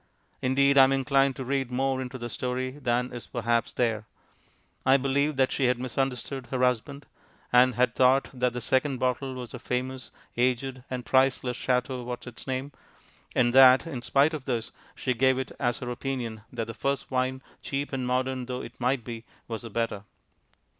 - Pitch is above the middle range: No, low, 130 Hz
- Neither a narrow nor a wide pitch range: No, narrow, 1.4 semitones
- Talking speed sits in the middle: Yes, average, 180 wpm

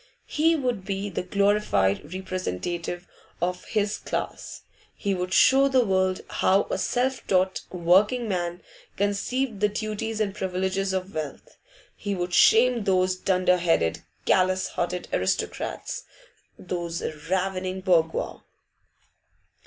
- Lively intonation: No, narrow, 2.4 semitones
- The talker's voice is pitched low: No, high, 190 Hz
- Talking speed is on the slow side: Yes, slow, 120 wpm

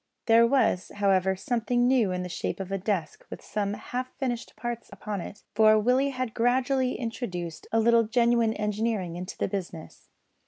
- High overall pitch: Yes, high, 220 Hz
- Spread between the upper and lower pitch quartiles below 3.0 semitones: No, average, 3.8 semitones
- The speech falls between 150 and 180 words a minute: Yes, average, 170 wpm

